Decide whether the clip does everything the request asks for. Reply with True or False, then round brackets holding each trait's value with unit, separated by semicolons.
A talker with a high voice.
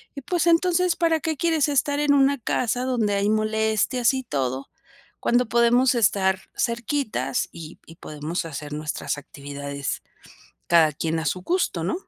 True (220 Hz)